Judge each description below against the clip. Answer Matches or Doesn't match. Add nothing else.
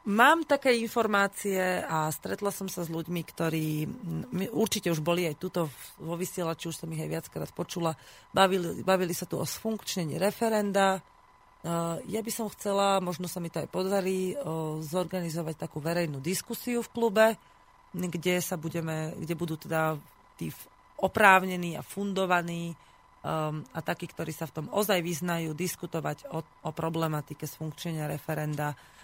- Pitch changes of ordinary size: Matches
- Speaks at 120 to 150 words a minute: Matches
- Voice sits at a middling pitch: Matches